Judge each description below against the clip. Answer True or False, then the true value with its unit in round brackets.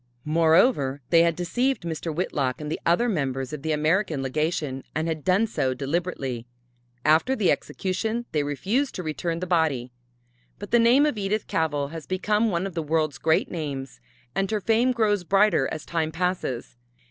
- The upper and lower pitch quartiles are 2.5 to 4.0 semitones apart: False (4.9 semitones)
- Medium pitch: True (165 Hz)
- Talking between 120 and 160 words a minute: False (175 wpm)